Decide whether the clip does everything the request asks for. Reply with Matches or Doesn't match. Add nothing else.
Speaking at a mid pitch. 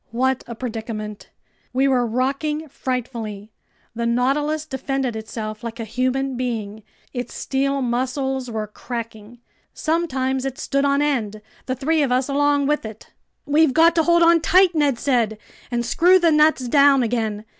Doesn't match